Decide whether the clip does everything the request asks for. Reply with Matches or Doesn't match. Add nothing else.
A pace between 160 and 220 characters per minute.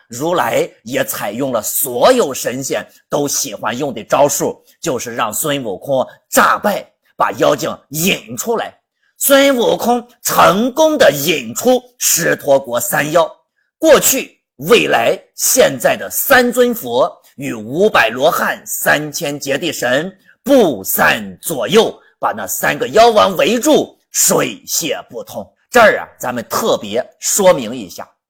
Matches